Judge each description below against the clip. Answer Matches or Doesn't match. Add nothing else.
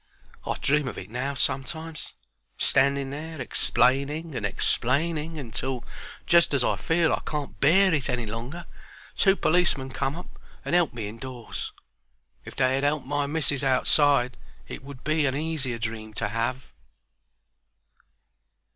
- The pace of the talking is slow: Doesn't match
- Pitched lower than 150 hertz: Matches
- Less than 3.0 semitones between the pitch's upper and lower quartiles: Doesn't match